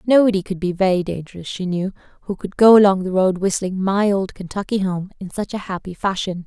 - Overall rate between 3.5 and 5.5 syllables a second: No, 5.8 syllables/s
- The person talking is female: Yes, female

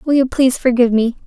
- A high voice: Yes, very high, 250 Hz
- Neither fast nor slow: No, fast, 235 wpm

